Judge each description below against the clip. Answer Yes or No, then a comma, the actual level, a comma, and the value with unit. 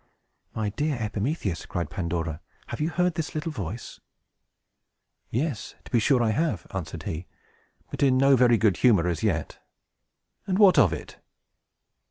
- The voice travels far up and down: Yes, wide, 8.5 semitones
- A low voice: Yes, low, 115 Hz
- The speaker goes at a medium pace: Yes, average, 155 wpm